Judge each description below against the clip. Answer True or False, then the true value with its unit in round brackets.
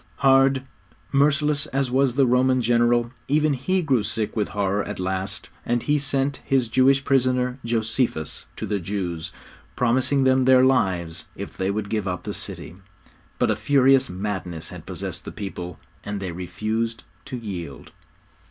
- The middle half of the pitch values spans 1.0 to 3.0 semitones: False (5.2 semitones)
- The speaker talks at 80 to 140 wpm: False (160 wpm)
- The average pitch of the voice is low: True (120 Hz)